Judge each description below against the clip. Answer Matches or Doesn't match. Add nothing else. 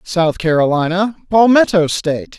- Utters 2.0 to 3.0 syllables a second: Doesn't match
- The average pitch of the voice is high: Doesn't match